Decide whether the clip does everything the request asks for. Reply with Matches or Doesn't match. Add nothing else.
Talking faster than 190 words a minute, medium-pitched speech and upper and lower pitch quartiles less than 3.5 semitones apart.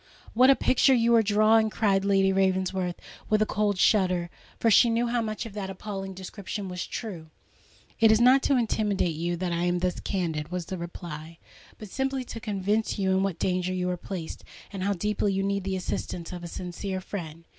Doesn't match